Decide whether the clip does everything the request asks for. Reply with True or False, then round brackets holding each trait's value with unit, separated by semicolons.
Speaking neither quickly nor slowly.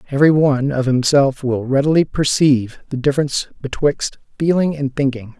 True (145 wpm)